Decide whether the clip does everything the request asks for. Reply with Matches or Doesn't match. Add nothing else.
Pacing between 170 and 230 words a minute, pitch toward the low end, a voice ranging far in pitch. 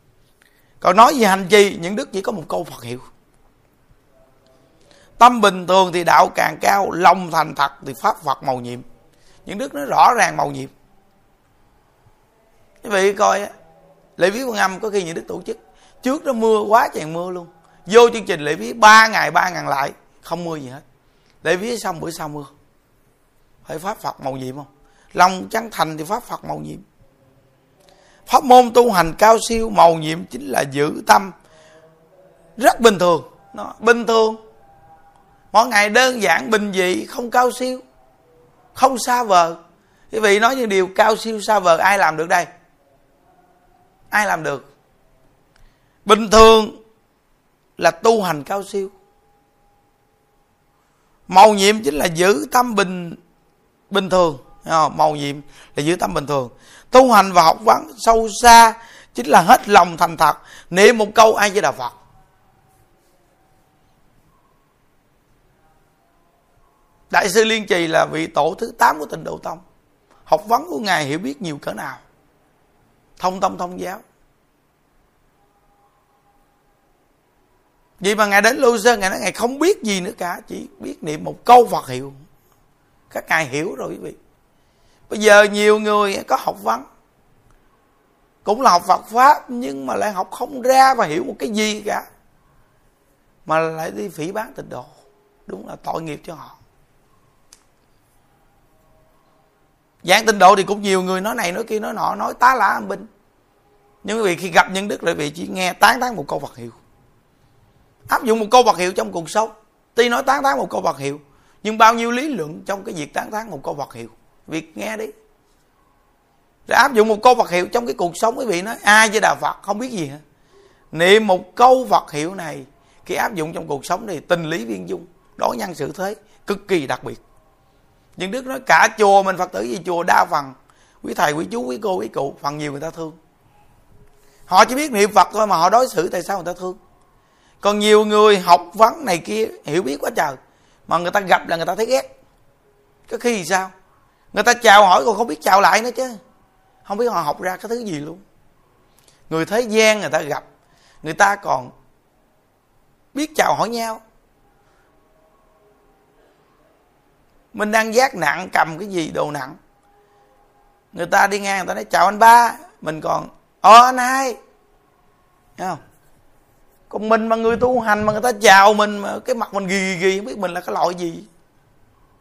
Doesn't match